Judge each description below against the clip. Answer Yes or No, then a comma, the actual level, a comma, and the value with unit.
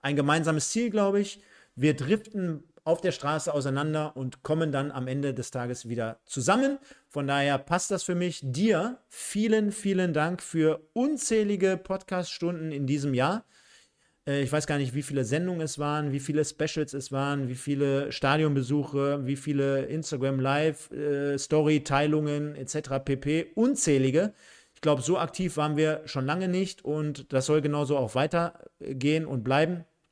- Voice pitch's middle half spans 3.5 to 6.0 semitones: Yes, average, 3.8 semitones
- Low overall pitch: No, medium, 150 Hz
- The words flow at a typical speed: Yes, average, 150 wpm